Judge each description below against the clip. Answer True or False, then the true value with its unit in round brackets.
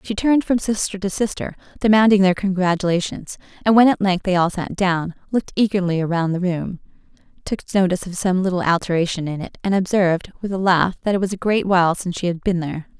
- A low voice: False (185 Hz)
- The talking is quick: True (210 wpm)